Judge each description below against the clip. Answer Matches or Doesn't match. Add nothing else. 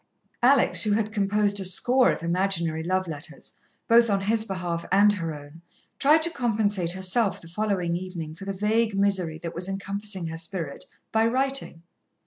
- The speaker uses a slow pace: Doesn't match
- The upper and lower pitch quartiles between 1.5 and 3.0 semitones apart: Doesn't match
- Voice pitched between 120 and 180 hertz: Doesn't match